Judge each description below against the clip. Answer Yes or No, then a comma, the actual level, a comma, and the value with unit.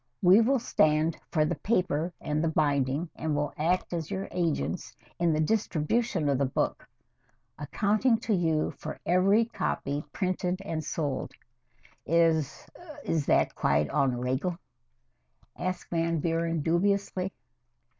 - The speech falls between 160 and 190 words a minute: No, slow, 135 wpm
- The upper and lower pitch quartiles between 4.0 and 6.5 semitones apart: No, average, 3.4 semitones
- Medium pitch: Yes, medium, 165 Hz